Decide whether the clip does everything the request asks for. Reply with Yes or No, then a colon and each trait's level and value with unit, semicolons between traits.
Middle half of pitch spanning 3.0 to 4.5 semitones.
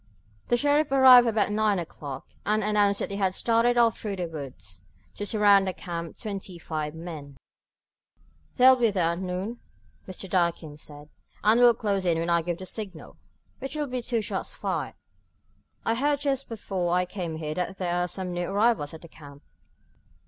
No: average, 5.2 semitones